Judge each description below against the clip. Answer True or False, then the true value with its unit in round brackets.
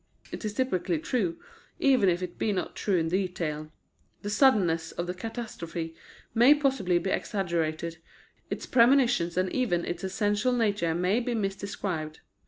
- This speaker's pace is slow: False (150 wpm)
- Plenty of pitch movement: False (4.9 semitones)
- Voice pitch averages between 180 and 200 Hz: True (190 Hz)